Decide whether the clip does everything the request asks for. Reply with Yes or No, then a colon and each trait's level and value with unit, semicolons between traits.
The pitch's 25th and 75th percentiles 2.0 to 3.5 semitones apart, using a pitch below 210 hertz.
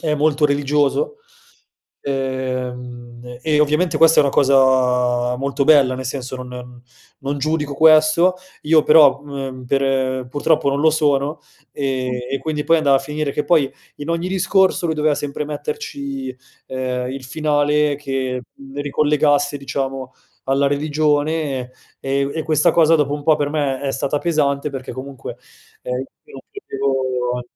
Yes: narrow, 2.5 semitones; medium, 140 Hz